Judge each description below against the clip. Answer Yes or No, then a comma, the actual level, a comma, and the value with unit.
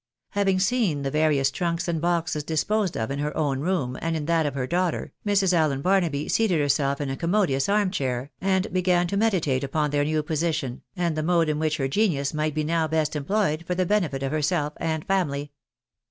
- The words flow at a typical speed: No, fast, 210 wpm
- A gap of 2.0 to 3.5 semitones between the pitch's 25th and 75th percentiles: No, average, 3.9 semitones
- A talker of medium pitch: Yes, medium, 160 Hz